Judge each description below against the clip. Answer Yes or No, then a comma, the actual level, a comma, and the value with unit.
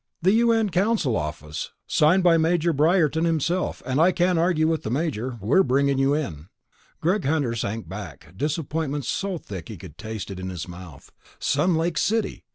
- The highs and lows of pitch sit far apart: Yes, wide, 7.8 semitones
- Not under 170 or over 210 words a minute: Yes, average, 175 wpm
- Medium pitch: Yes, medium, 150 Hz